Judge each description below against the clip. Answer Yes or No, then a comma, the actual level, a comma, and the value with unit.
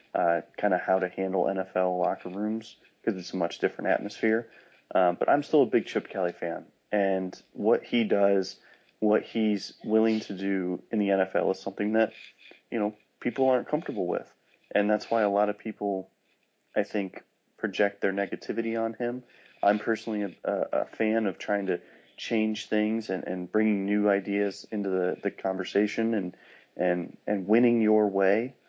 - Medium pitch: No, low, 105 Hz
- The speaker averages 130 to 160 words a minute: No, average, 175 wpm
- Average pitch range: No, narrow, 2.3 semitones